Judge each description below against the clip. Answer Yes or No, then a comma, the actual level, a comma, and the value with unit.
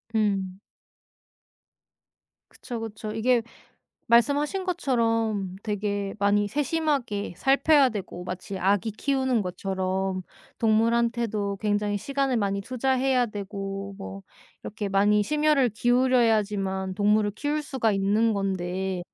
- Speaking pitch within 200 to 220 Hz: Yes, high, 215 Hz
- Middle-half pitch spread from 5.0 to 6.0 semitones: No, average, 4.1 semitones